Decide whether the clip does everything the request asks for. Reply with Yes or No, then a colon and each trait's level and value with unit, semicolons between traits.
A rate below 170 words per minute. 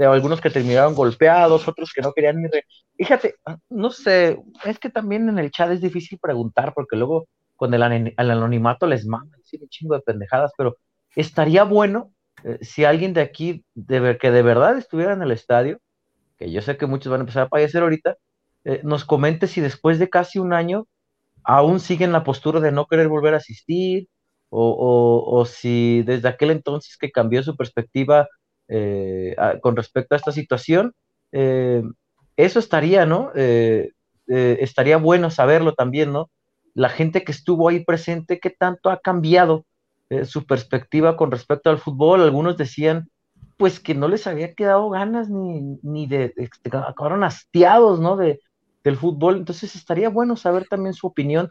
No: average, 175 wpm